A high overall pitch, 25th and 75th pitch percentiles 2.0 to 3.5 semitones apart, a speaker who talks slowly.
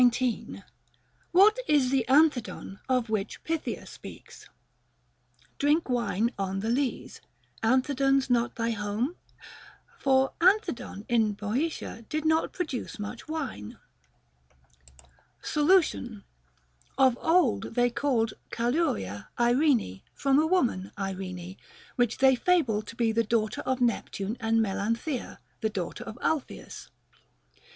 No: high, 245 Hz; average, 4.8 semitones; slow, 115 wpm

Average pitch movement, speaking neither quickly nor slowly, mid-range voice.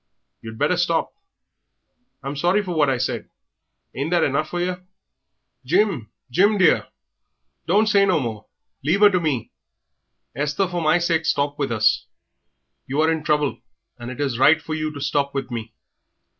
Yes: average, 4.3 semitones; average, 170 wpm; medium, 155 Hz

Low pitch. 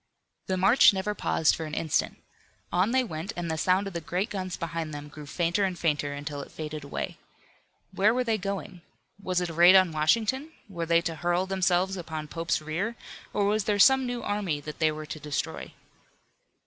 No: medium, 175 Hz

